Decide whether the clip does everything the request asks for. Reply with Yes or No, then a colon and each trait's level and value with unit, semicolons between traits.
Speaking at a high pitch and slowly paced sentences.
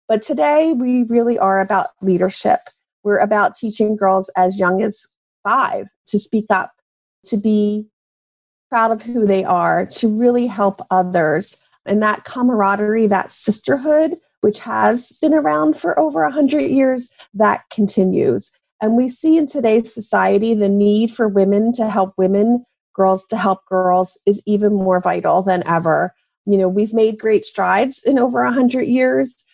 No: high, 210 Hz; average, 155 wpm